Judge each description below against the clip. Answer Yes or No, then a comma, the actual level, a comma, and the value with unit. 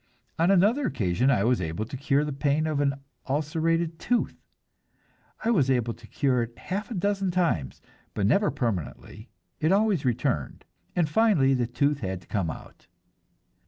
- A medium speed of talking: Yes, average, 165 wpm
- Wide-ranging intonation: Yes, wide, 6.6 semitones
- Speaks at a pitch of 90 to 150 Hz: Yes, medium, 140 Hz